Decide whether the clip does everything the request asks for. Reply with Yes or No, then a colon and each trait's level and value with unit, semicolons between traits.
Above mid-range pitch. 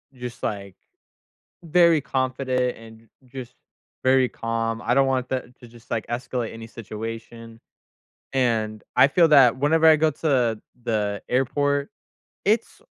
No: low, 125 Hz